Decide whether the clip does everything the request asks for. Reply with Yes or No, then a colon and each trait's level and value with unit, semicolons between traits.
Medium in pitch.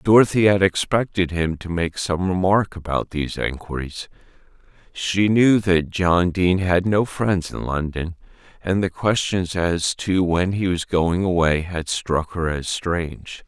No: very low, 90 Hz